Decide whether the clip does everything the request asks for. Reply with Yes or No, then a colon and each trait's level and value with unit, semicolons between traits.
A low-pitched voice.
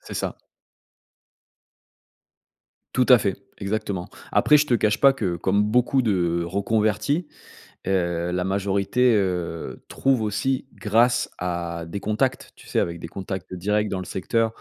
Yes: low, 100 Hz